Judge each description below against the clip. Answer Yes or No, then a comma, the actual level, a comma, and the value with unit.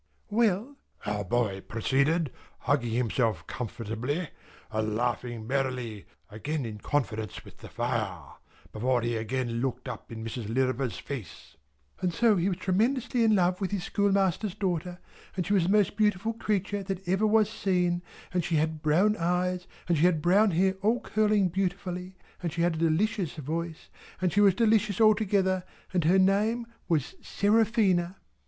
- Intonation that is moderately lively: No, wide, 7.8 semitones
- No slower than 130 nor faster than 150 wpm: No, average, 160 wpm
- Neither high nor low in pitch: Yes, medium, 175 Hz